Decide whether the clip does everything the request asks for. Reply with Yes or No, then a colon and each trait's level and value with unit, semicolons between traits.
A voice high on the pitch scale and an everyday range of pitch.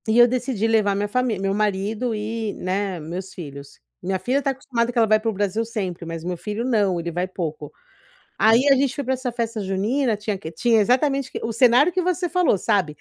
Yes: high, 215 Hz; average, 4.6 semitones